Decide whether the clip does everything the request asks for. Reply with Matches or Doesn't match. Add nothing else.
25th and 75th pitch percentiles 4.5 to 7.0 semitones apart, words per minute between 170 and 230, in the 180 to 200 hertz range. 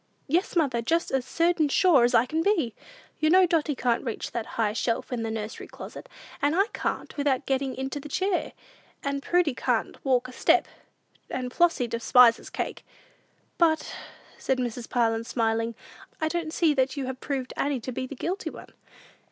Doesn't match